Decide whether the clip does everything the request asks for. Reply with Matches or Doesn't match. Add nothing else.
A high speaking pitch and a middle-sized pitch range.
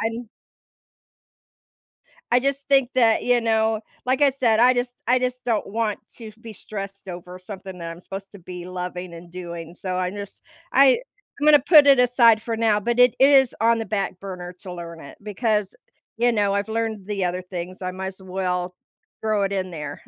Matches